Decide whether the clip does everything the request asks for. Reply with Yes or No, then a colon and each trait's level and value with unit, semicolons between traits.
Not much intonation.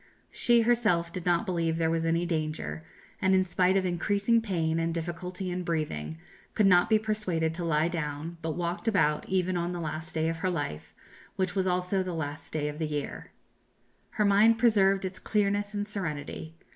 No: average, 3.2 semitones